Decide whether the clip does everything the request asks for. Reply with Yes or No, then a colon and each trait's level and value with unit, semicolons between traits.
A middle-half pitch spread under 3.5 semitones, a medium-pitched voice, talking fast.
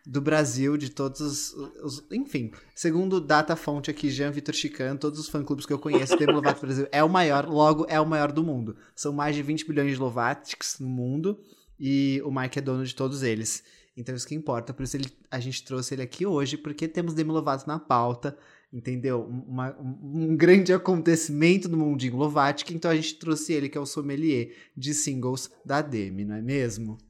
Yes: average, 2.8 semitones; medium, 145 Hz; fast, 205 wpm